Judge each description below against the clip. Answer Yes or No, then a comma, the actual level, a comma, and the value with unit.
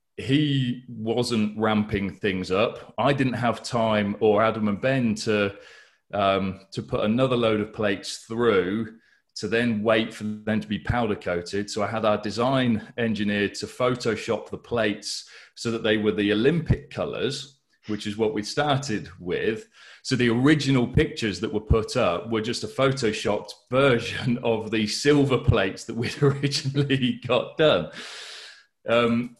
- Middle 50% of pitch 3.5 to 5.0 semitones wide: No, average, 2.8 semitones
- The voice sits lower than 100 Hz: No, low, 110 Hz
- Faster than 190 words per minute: No, average, 155 wpm